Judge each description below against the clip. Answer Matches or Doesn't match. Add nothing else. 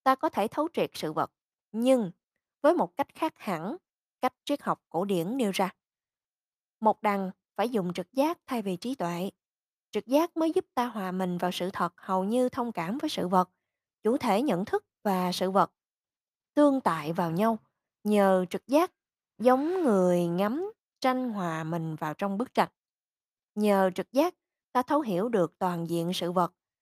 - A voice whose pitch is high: Matches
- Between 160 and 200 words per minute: Matches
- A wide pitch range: Matches